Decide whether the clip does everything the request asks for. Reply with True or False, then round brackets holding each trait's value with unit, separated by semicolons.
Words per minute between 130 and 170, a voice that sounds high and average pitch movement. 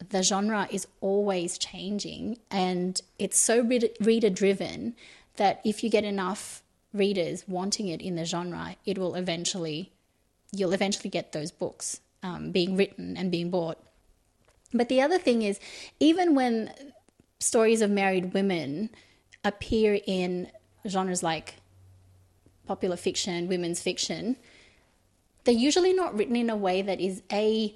True (135 wpm; 195 Hz; 3.7 semitones)